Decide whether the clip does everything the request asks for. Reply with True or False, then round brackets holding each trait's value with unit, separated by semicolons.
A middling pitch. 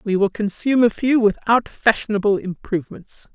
False (210 Hz)